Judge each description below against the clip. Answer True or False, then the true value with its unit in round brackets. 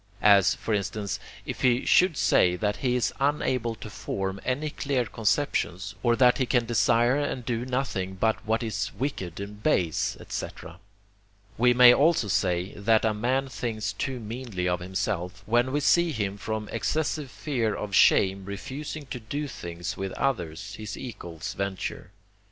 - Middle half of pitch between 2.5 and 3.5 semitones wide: False (4.7 semitones)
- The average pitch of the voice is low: True (110 Hz)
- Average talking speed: True (165 wpm)